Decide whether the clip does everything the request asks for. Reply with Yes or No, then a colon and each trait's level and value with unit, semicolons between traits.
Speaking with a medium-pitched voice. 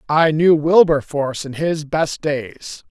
Yes: medium, 150 Hz